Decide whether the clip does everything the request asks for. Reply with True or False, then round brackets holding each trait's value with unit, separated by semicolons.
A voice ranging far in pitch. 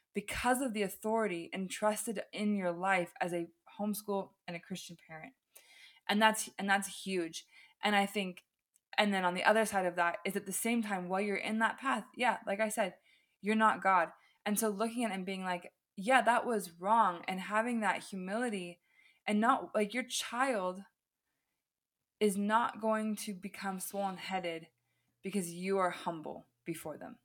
False (3.1 semitones)